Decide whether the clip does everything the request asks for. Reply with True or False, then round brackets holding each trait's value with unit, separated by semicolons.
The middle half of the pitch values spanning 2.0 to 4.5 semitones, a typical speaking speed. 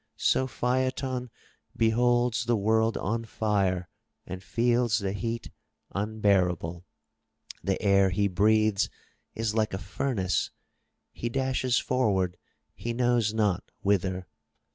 False (3.7 semitones; 115 wpm)